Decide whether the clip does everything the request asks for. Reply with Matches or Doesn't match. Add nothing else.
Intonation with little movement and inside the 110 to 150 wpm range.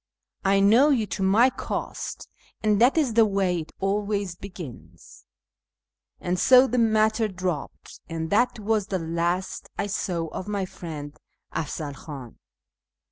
Doesn't match